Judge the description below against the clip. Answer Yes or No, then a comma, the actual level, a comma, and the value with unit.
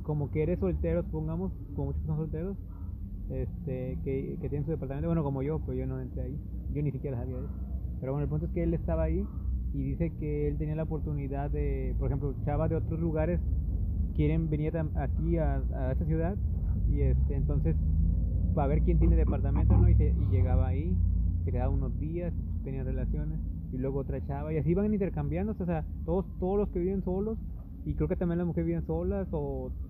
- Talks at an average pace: No, fast, 205 wpm